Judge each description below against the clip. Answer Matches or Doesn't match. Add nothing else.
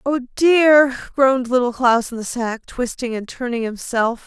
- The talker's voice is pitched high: Matches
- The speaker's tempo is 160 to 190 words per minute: Matches